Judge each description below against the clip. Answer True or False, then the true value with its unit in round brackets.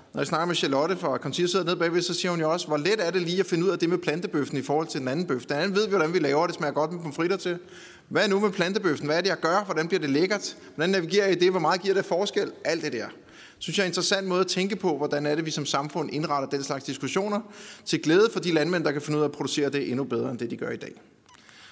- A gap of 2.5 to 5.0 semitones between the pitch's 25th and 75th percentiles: True (4.2 semitones)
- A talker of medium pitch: True (170 Hz)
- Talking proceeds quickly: True (315 wpm)